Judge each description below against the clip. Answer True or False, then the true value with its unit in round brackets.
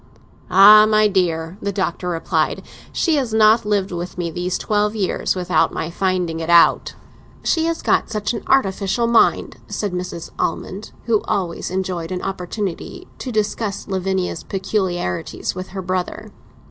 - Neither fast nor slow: True (150 wpm)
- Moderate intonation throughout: True (3.0 semitones)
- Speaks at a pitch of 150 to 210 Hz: True (190 Hz)